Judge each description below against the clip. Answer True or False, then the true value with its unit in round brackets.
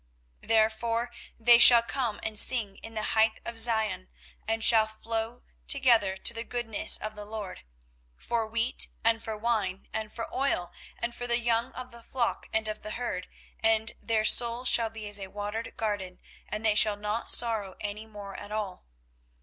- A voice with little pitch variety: True (1.9 semitones)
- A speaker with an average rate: True (180 wpm)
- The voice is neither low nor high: False (220 Hz)